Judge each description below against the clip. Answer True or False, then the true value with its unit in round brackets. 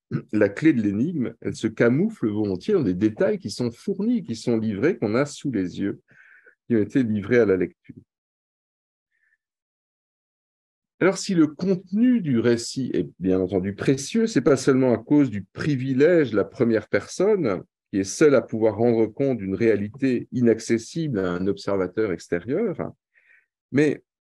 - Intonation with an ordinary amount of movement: False (6.3 semitones)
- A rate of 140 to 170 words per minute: True (160 wpm)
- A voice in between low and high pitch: False (120 Hz)